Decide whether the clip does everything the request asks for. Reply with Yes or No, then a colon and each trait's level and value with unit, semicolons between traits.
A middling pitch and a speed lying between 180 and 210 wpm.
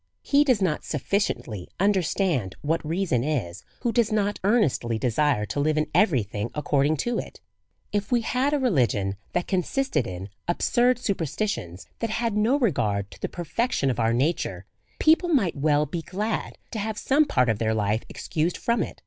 Yes: medium, 165 Hz; average, 185 wpm